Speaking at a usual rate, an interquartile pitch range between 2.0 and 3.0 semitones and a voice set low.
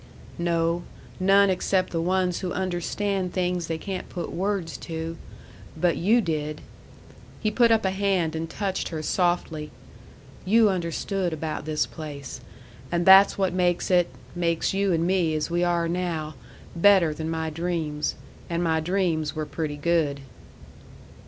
No: average, 150 wpm; average, 2.7 semitones; medium, 175 Hz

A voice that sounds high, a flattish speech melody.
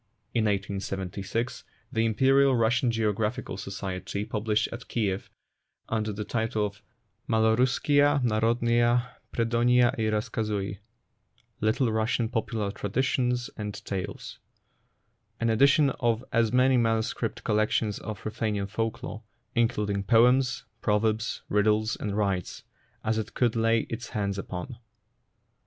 No: low, 110 Hz; narrow, 2.3 semitones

